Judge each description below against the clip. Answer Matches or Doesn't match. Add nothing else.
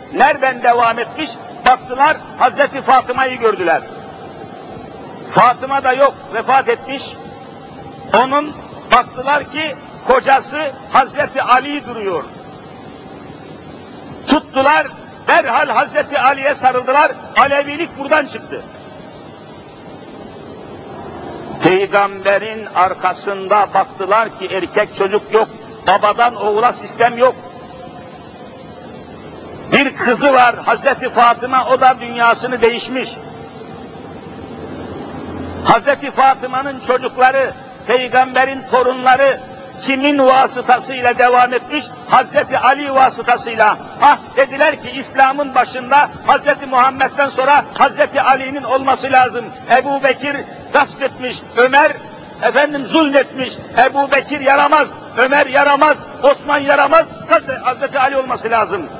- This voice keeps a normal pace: Doesn't match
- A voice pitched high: Matches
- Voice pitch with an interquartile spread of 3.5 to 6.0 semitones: Doesn't match